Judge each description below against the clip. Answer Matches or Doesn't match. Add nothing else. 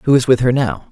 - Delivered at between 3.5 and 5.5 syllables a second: Doesn't match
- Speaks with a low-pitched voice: Matches